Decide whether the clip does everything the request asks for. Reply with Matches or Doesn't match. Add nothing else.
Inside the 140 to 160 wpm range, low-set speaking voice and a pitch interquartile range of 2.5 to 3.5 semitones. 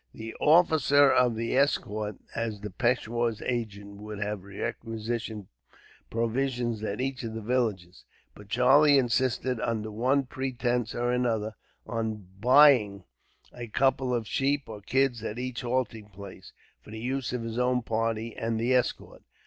Matches